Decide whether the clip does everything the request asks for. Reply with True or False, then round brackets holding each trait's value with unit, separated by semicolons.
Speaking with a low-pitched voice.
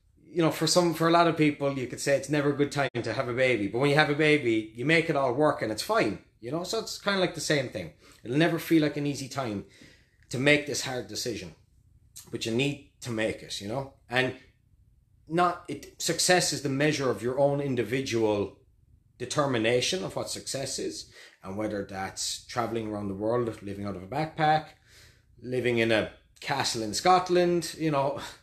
True (130 Hz)